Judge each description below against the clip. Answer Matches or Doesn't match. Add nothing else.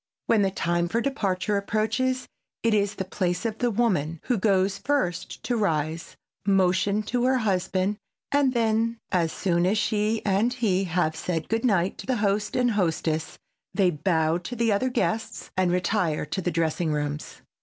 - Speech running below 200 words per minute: Matches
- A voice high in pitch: Matches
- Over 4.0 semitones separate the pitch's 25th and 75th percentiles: Matches